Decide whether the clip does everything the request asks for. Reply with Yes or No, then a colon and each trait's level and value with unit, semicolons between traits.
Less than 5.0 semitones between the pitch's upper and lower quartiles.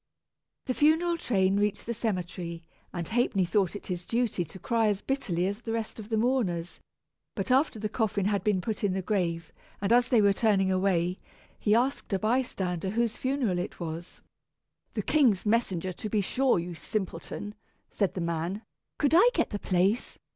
Yes: average, 4.4 semitones